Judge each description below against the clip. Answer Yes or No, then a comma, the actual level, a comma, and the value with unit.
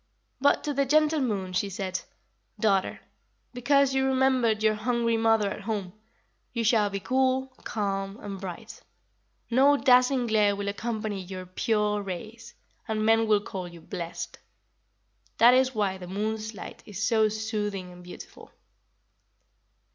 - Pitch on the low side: No, high, 215 Hz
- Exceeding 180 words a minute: No, average, 145 wpm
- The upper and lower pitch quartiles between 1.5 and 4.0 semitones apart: Yes, average, 3.7 semitones